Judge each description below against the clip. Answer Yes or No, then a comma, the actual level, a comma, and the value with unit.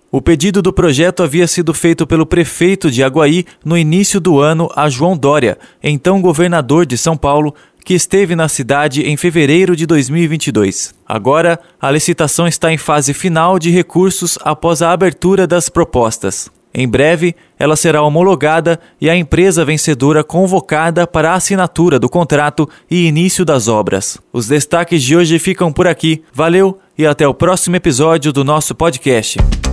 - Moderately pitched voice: Yes, medium, 165 Hz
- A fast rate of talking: No, average, 160 wpm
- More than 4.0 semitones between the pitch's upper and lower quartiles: No, average, 2.8 semitones